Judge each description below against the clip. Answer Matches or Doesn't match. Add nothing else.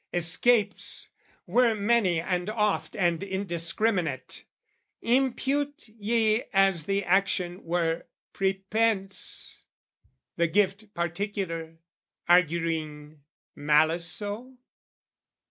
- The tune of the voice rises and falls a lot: Doesn't match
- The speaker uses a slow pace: Matches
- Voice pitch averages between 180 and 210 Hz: Matches